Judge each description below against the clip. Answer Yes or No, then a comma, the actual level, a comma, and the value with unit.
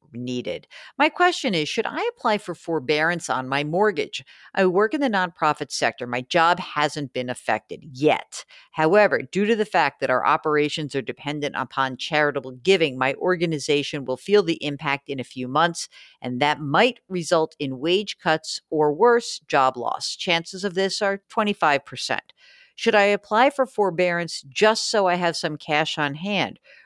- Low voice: No, medium, 165 Hz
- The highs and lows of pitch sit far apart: Yes, wide, 5.8 semitones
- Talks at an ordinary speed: Yes, average, 170 wpm